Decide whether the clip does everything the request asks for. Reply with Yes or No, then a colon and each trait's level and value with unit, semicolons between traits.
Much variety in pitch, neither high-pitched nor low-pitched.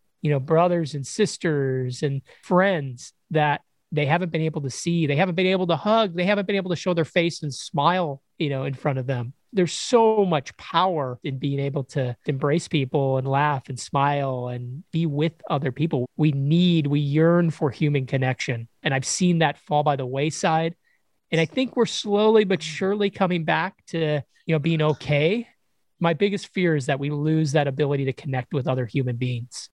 No: average, 4.0 semitones; medium, 155 Hz